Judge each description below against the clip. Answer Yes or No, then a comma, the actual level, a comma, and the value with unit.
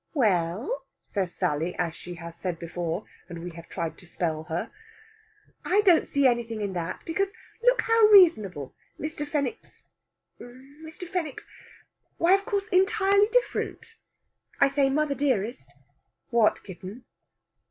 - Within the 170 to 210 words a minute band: No, average, 140 wpm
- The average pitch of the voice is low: No, high, 245 Hz